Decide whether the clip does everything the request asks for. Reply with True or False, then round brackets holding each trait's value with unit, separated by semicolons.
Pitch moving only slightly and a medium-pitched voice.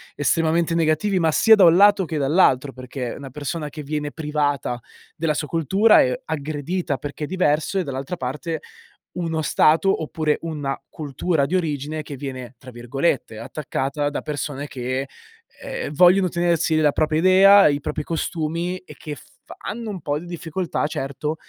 False (3.3 semitones; 155 Hz)